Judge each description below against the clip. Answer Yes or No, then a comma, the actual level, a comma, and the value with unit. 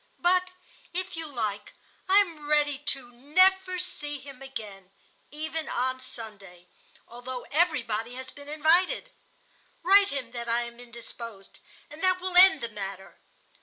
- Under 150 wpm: Yes, average, 140 wpm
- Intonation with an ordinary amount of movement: No, wide, 6.8 semitones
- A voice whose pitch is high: Yes, very high, 275 Hz